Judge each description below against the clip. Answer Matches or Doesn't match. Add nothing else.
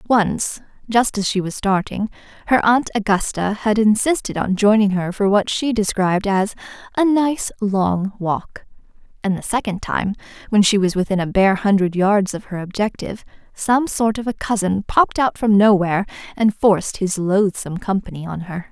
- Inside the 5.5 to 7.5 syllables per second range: Doesn't match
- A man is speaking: Doesn't match